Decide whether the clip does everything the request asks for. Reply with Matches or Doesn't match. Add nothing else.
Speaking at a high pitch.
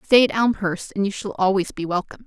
Matches